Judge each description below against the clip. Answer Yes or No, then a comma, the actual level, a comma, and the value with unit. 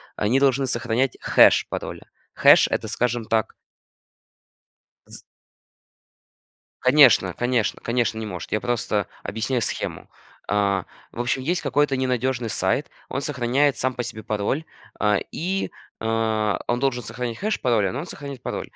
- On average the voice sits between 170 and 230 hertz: No, low, 120 Hz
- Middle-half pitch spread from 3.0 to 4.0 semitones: Yes, average, 3.3 semitones